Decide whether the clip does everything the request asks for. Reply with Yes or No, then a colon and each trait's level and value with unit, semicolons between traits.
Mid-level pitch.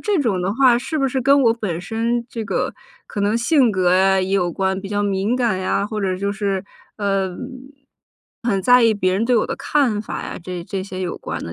No: high, 205 Hz